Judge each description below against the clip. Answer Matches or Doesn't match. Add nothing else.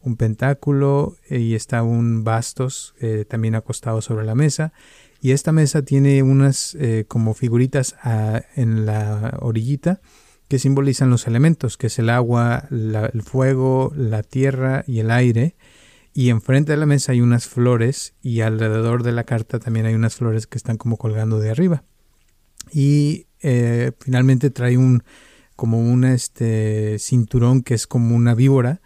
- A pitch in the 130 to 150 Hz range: Doesn't match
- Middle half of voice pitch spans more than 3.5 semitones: Doesn't match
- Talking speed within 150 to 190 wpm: Matches